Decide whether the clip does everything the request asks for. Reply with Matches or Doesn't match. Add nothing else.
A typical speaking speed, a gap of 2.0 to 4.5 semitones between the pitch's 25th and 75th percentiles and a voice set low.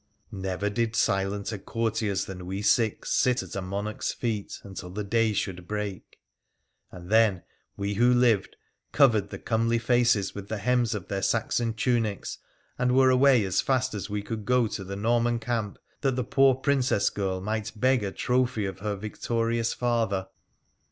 Matches